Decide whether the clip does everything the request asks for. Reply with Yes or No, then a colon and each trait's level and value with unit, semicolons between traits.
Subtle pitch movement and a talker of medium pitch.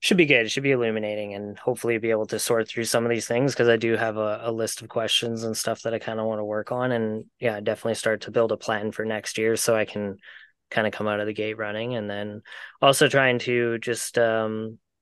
No: narrow, 1.5 semitones; low, 110 Hz